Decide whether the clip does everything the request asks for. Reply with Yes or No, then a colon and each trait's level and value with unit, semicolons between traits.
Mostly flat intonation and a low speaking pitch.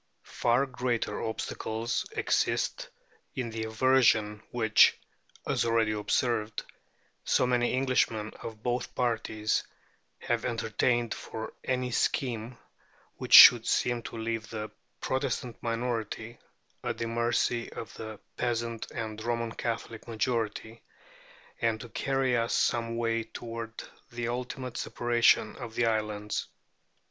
Yes: narrow, 1.6 semitones; low, 115 Hz